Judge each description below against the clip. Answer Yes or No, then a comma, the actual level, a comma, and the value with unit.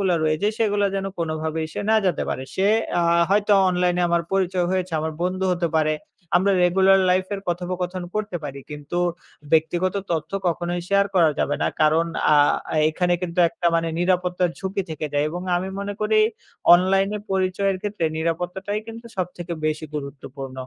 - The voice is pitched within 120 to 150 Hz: No, medium, 180 Hz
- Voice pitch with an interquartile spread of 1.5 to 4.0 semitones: Yes, average, 2.9 semitones